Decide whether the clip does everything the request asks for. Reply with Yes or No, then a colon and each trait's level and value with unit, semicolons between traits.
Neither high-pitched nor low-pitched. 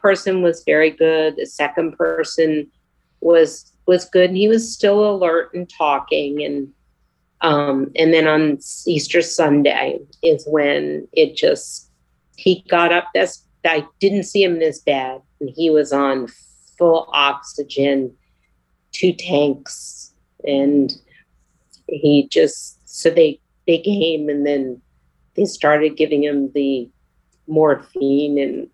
Yes: medium, 150 Hz